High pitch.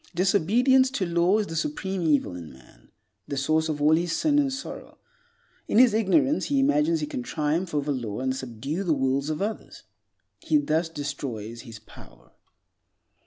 No: medium, 165 Hz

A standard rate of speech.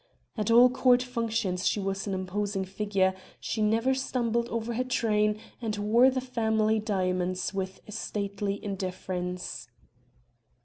No: slow, 130 wpm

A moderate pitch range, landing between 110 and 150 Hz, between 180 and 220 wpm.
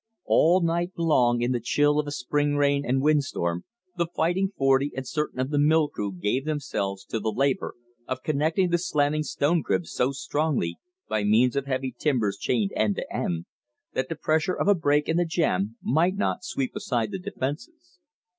Yes: average, 4.6 semitones; medium, 140 Hz; average, 190 wpm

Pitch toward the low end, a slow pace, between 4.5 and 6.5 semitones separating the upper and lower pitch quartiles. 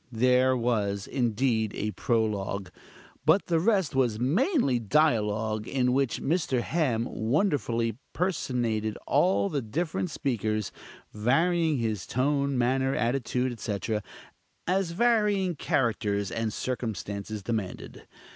Yes: low, 125 Hz; slow, 110 wpm; average, 5.2 semitones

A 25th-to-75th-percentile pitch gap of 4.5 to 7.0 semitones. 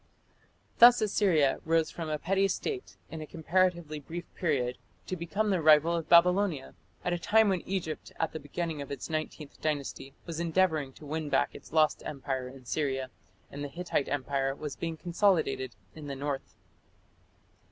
No: average, 3.6 semitones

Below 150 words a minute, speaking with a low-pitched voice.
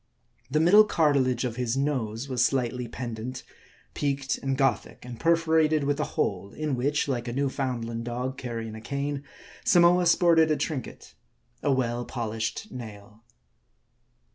Yes: average, 140 wpm; low, 130 Hz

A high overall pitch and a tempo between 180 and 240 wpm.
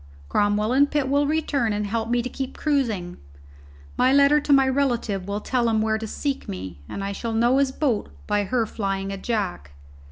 Yes: high, 230 Hz; average, 200 wpm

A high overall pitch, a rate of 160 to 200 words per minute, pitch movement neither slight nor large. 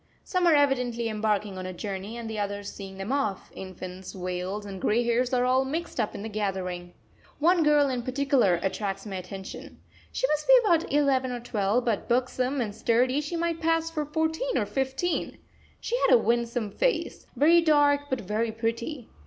No: high, 240 Hz; average, 185 wpm; wide, 6.1 semitones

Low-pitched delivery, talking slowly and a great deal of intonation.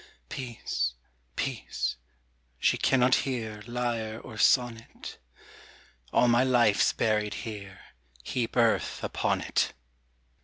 No: low, 115 Hz; slow, 100 wpm; narrow, 2.4 semitones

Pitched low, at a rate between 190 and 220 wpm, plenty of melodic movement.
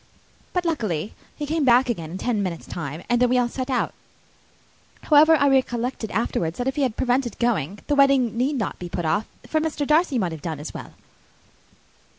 No: high, 245 Hz; fast, 205 wpm; wide, 6.5 semitones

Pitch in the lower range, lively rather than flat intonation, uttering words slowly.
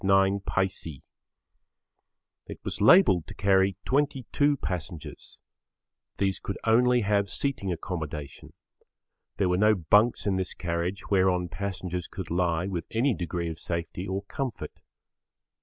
No: very low, 95 Hz; average, 2.9 semitones; slow, 125 wpm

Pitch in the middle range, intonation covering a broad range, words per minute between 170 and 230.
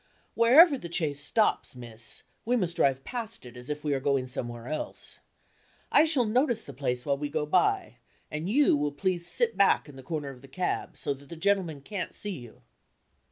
Yes: medium, 155 Hz; wide, 7.7 semitones; fast, 205 wpm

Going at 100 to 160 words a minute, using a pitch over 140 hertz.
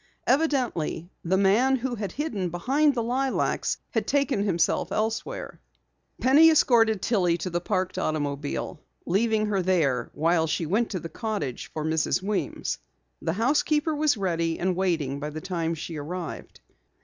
Yes: average, 150 wpm; high, 190 Hz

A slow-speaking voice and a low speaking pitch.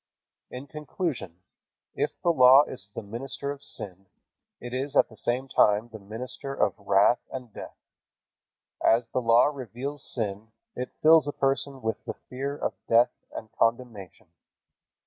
No: average, 150 wpm; low, 125 Hz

